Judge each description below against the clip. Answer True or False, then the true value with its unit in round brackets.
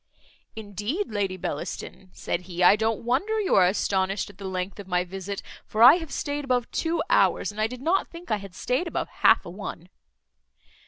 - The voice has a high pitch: True (205 Hz)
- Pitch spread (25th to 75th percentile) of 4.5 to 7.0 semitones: True (5.5 semitones)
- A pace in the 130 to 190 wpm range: False (200 wpm)